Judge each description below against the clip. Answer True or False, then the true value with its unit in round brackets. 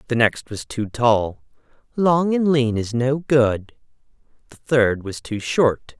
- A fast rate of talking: False (160 wpm)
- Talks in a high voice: False (125 Hz)